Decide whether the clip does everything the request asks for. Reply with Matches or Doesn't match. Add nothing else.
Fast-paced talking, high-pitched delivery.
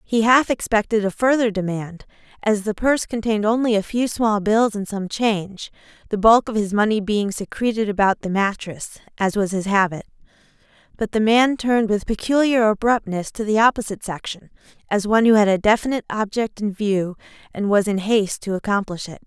Doesn't match